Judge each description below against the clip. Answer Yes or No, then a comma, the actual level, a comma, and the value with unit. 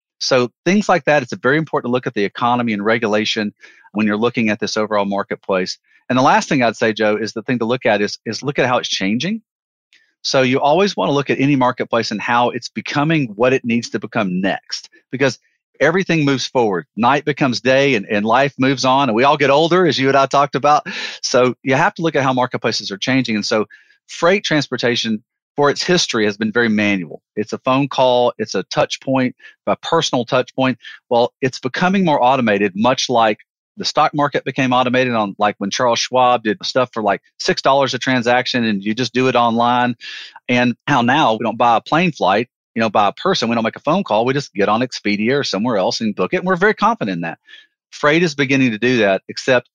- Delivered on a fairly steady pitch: No, average, 4.3 semitones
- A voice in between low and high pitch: No, low, 125 Hz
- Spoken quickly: Yes, fast, 230 wpm